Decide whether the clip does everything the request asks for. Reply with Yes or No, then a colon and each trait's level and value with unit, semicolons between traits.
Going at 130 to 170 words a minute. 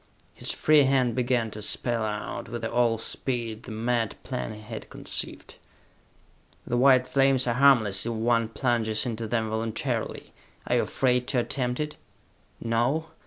Yes: average, 155 wpm